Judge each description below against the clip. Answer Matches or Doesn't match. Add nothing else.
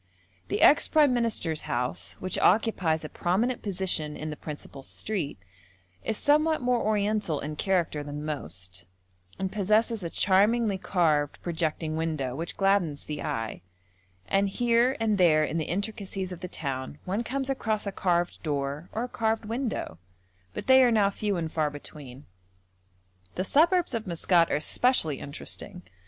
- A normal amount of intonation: Doesn't match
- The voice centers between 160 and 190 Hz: Matches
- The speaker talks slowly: Doesn't match